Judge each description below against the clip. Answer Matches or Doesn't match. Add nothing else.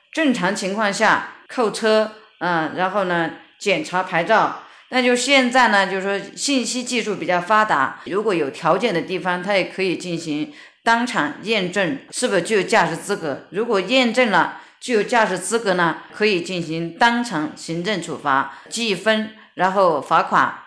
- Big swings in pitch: Doesn't match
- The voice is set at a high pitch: Matches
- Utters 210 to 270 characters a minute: Matches